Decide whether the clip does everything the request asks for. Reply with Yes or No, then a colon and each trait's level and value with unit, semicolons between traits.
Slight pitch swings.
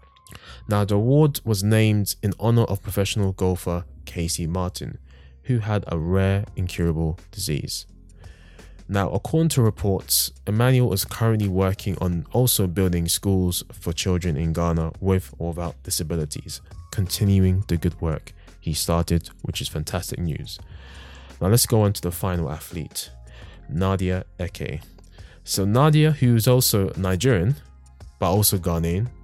No: average, 3.5 semitones